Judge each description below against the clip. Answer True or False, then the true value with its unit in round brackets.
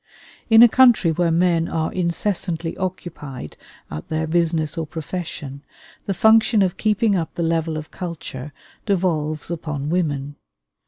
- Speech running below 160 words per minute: True (140 wpm)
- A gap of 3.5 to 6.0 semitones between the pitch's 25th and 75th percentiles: False (3.1 semitones)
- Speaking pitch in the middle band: True (165 Hz)